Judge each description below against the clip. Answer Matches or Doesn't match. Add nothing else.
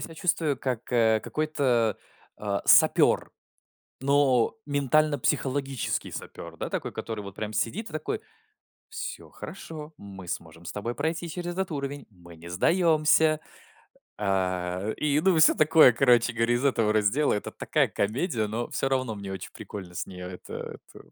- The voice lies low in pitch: Matches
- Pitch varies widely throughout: Matches